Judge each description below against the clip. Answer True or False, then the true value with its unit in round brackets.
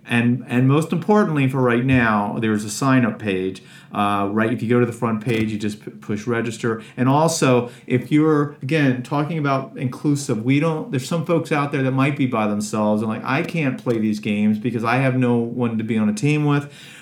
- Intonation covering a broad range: False (4.5 semitones)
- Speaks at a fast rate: True (220 wpm)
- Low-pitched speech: True (125 Hz)